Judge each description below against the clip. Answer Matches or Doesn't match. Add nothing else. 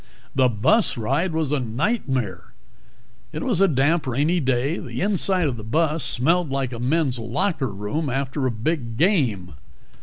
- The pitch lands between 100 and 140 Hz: Matches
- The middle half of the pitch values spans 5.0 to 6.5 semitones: Matches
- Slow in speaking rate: Doesn't match